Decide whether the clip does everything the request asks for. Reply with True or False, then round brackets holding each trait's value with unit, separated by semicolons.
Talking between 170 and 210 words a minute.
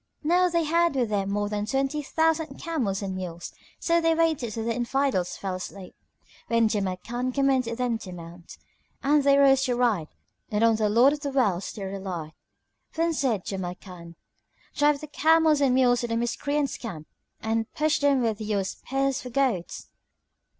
True (175 wpm)